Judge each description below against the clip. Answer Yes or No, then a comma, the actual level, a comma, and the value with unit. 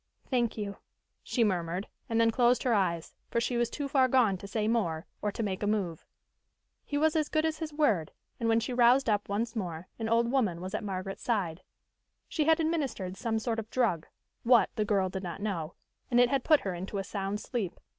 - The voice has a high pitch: Yes, high, 220 Hz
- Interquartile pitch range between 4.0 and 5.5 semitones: Yes, average, 4.3 semitones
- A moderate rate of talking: No, fast, 220 wpm